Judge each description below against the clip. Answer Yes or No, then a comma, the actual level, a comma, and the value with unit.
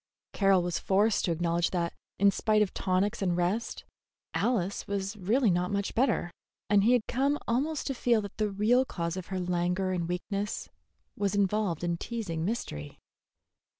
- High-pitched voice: Yes, high, 195 Hz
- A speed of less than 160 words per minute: No, average, 170 wpm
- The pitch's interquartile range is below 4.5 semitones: Yes, average, 3.5 semitones